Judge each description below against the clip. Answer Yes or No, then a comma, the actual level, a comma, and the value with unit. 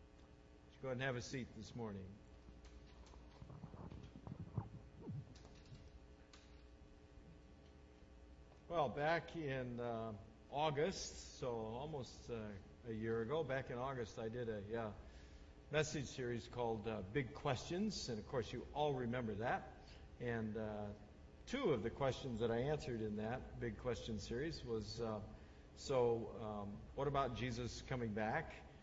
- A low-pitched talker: Yes, low, 110 Hz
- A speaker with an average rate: No, slow, 130 wpm